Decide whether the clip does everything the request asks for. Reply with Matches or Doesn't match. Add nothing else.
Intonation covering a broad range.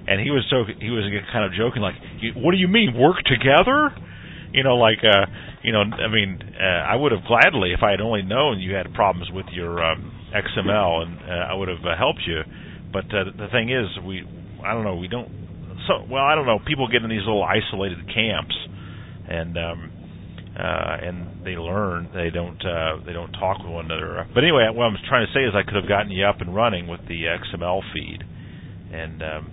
Doesn't match